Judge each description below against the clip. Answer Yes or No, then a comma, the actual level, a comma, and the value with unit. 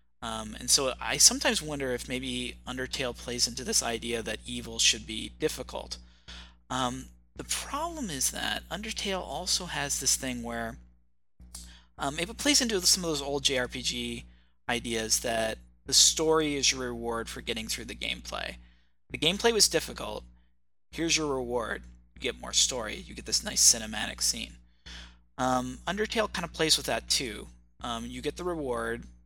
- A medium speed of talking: Yes, average, 165 wpm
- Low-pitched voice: Yes, low, 120 Hz